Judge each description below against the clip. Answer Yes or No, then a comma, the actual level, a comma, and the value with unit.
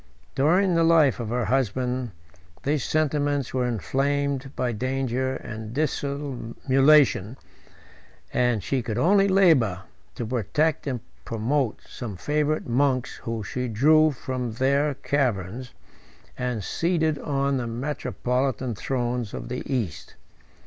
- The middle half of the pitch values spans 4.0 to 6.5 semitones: No, average, 3.3 semitones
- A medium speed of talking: No, slow, 120 wpm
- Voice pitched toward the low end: Yes, low, 130 Hz